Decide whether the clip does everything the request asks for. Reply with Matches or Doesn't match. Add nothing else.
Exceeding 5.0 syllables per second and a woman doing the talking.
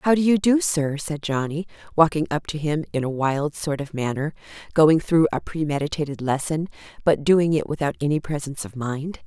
Matches